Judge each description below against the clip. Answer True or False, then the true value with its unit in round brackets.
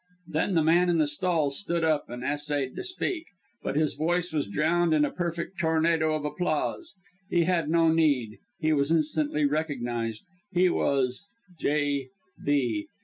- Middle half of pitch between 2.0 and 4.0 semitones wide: True (2.9 semitones)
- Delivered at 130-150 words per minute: False (160 wpm)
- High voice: False (155 Hz)